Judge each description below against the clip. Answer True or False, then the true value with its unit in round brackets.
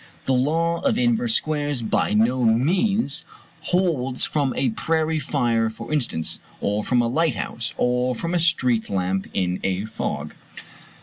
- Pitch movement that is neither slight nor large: False (6.4 semitones)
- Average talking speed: True (145 wpm)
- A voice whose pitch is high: False (130 Hz)